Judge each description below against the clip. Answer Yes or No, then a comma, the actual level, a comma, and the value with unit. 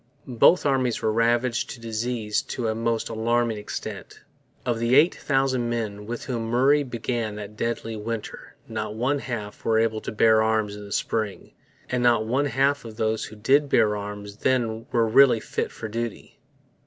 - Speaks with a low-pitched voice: Yes, low, 115 Hz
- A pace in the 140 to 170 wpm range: No, average, 180 wpm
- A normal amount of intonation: No, narrow, 2.0 semitones